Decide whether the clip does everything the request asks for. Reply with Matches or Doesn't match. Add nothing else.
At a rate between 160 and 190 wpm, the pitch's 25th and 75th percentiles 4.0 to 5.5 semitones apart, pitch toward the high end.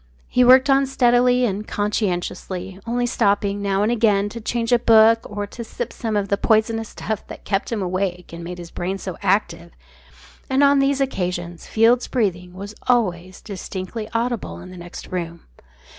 Matches